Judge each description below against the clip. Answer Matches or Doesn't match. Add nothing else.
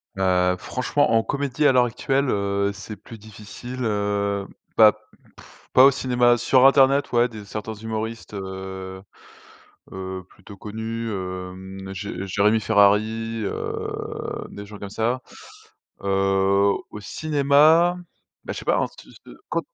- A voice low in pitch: Matches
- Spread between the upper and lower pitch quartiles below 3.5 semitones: Doesn't match